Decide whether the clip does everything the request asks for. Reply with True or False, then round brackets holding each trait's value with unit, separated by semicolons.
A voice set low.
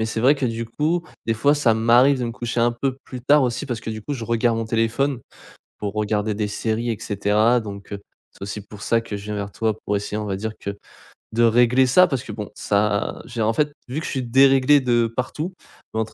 True (115 Hz)